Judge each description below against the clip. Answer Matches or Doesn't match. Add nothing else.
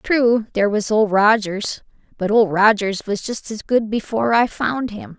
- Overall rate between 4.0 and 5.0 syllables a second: Matches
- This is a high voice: Matches